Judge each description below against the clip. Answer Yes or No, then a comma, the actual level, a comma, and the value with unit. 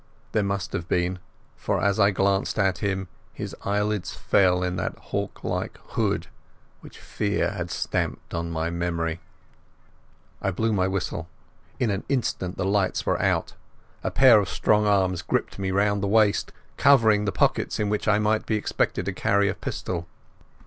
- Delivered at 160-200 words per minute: Yes, average, 175 wpm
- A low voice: Yes, low, 100 Hz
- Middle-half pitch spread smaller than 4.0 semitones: Yes, narrow, 2.4 semitones